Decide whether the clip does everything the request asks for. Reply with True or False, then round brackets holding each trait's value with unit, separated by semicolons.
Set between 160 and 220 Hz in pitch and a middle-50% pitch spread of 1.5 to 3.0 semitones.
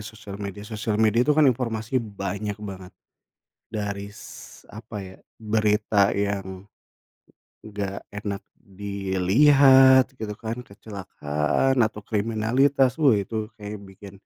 False (105 Hz; 2.4 semitones)